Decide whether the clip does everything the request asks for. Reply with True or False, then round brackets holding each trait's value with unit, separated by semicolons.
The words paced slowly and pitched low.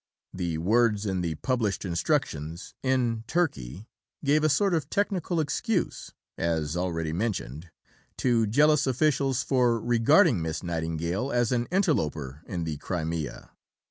True (130 wpm; 110 Hz)